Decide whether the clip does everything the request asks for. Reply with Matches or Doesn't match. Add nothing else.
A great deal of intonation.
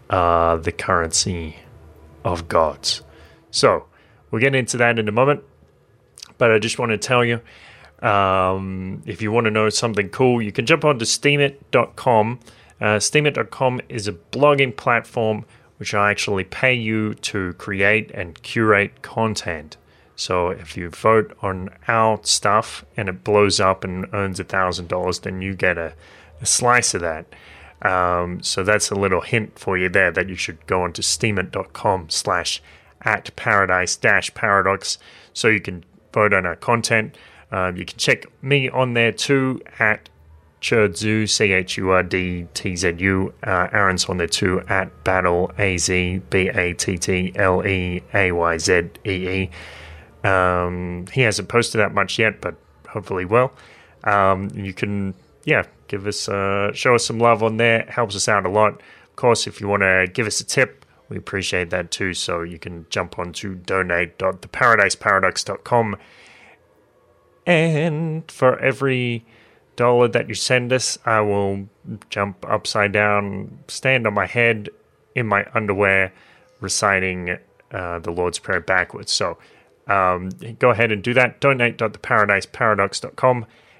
Doesn't match